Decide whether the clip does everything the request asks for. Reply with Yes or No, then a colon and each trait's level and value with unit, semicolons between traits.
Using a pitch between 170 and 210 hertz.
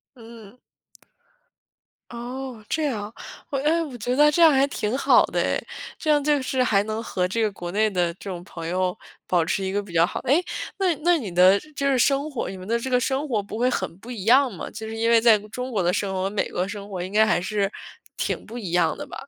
No: high, 225 Hz